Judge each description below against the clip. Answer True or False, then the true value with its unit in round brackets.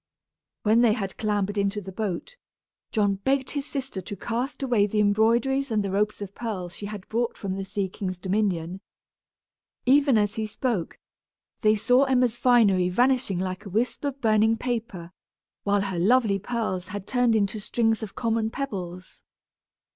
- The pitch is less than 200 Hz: False (215 Hz)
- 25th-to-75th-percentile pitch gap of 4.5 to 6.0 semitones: False (3.6 semitones)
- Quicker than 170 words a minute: False (165 wpm)